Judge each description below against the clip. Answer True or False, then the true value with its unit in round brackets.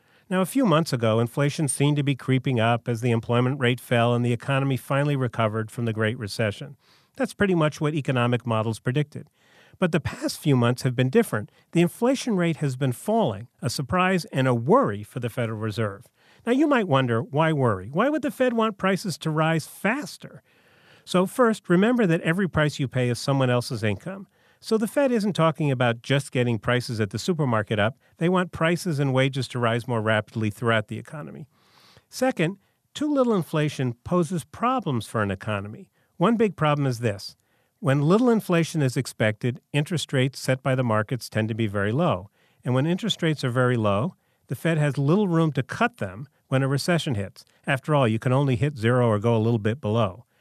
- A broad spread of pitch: True (6.2 semitones)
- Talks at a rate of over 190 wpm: True (200 wpm)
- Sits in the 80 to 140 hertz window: True (135 Hz)